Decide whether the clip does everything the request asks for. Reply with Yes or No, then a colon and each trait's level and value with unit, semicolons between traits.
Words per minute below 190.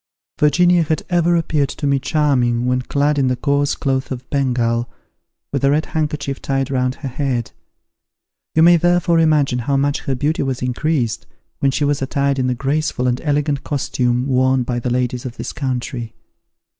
Yes: average, 180 wpm